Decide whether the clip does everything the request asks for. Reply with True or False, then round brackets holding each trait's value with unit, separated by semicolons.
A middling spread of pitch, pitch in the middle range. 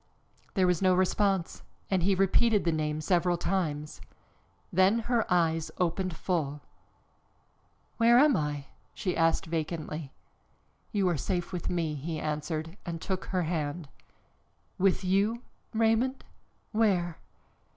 True (3.5 semitones; 180 Hz)